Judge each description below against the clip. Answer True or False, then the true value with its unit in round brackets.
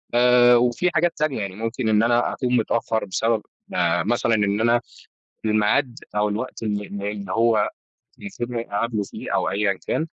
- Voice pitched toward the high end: False (115 Hz)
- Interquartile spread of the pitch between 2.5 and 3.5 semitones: True (2.8 semitones)